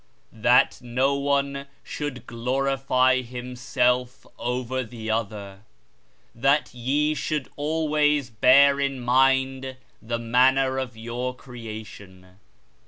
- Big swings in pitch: No, narrow, 2.5 semitones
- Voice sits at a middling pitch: No, low, 130 Hz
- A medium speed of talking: No, slow, 100 wpm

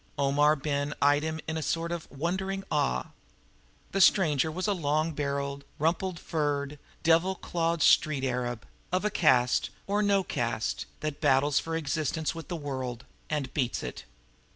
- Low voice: No, medium, 150 Hz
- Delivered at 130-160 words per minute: Yes, average, 155 wpm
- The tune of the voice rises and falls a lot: No, average, 3.1 semitones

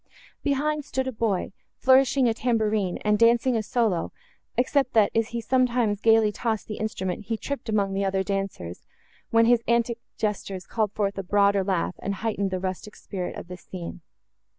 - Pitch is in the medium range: No, high, 215 Hz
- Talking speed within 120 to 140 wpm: No, average, 175 wpm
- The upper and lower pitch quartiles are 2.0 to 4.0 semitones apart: Yes, average, 3.3 semitones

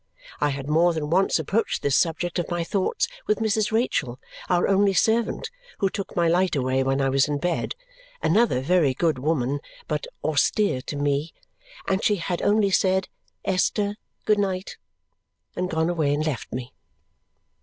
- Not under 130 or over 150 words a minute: No, average, 165 wpm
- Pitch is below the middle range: No, medium, 170 Hz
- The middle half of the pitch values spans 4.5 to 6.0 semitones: Yes, average, 5.2 semitones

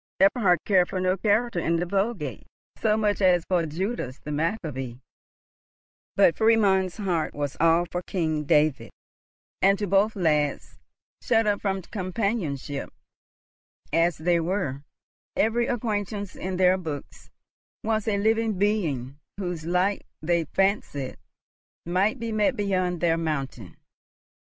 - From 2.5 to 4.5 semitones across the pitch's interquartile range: Yes, average, 4.2 semitones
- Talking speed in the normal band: No, slow, 130 wpm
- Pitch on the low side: No, medium, 185 Hz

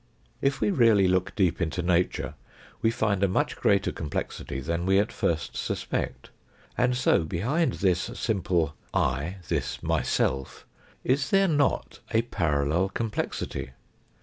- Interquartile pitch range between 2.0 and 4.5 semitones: No, wide, 5.6 semitones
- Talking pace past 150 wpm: No, average, 140 wpm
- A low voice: Yes, very low, 95 Hz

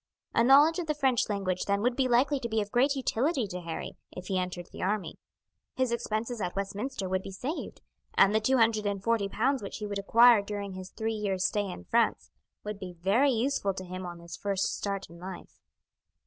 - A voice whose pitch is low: No, high, 205 Hz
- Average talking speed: No, fast, 220 wpm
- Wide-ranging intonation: No, average, 4.3 semitones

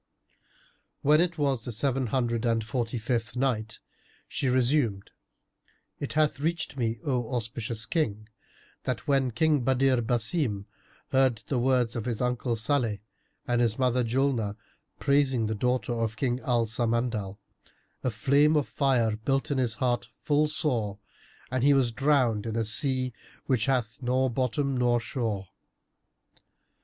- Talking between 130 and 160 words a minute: Yes, average, 145 wpm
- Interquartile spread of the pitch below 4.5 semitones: Yes, average, 3.0 semitones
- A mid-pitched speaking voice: No, low, 125 Hz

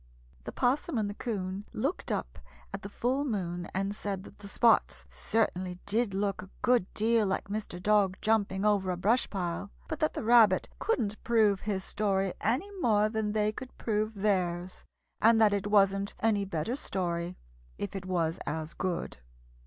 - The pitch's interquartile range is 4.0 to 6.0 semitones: No, average, 2.8 semitones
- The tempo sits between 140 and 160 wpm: No, average, 175 wpm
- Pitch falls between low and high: No, high, 205 Hz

